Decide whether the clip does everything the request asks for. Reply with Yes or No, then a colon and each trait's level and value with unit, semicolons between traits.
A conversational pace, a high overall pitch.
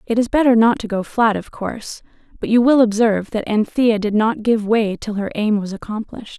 No: fast, 225 wpm; high, 220 Hz